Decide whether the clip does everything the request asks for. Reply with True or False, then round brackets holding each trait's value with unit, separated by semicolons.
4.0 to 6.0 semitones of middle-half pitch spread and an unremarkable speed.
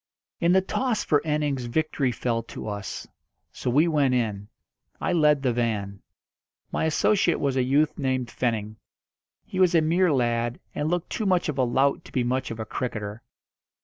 True (5.0 semitones; 180 wpm)